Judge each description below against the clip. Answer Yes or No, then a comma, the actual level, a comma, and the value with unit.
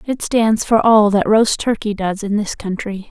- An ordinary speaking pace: No, fast, 210 wpm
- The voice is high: Yes, high, 210 Hz